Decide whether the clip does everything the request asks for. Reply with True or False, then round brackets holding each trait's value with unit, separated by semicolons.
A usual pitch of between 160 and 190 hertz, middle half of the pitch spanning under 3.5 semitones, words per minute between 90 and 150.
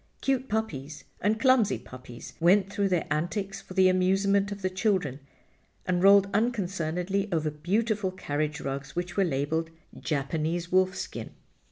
False (185 Hz; 4.2 semitones; 140 wpm)